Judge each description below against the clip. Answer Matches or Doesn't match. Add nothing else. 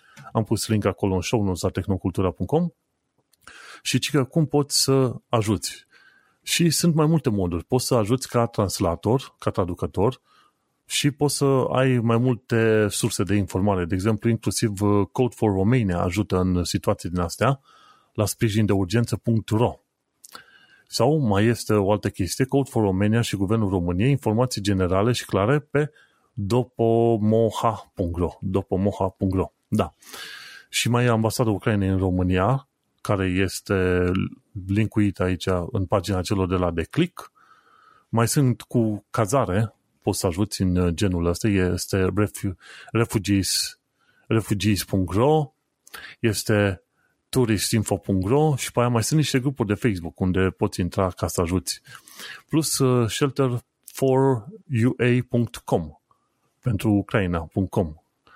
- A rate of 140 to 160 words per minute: Doesn't match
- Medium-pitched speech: Doesn't match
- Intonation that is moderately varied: Matches